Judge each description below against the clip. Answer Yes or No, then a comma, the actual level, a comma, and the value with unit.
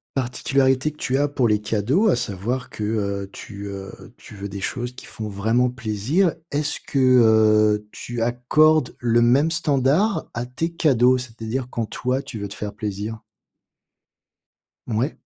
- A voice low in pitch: Yes, low, 120 Hz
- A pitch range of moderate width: Yes, average, 3.9 semitones